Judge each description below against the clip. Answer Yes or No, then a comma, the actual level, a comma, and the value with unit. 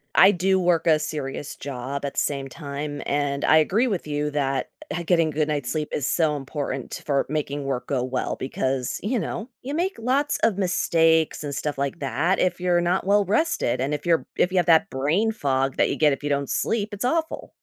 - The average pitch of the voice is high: No, medium, 150 Hz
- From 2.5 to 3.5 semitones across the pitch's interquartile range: No, average, 4.7 semitones